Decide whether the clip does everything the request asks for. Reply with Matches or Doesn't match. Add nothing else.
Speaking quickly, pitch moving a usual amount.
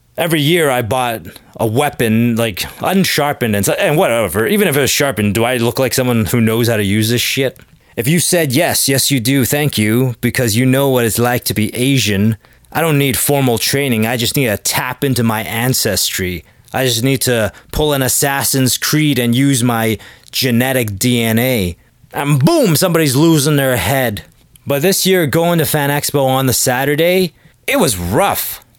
Doesn't match